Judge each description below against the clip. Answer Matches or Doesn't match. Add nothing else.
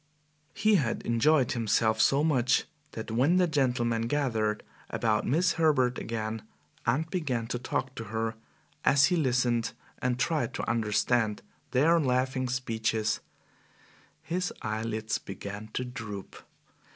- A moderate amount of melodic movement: Matches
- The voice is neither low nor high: Doesn't match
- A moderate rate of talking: Doesn't match